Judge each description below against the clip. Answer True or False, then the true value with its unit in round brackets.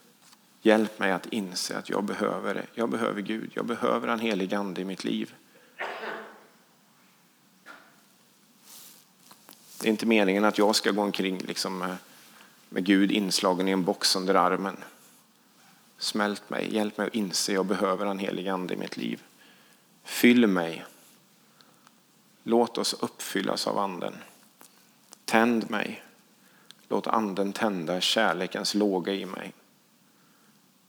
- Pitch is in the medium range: False (105 Hz)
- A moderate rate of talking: False (130 wpm)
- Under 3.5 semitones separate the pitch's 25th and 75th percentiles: True (3.1 semitones)